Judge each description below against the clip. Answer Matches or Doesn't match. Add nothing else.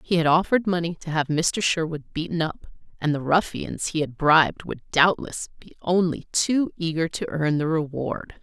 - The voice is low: Doesn't match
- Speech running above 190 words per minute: Doesn't match